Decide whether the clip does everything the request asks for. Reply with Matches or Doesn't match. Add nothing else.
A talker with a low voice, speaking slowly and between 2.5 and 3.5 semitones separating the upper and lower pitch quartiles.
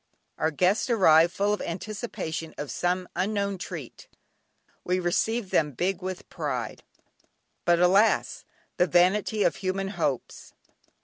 Doesn't match